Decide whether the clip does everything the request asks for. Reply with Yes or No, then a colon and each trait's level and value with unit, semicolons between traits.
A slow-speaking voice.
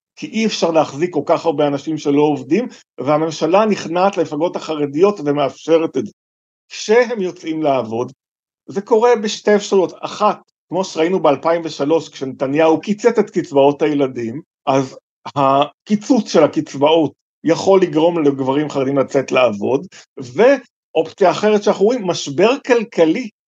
No: average, 125 wpm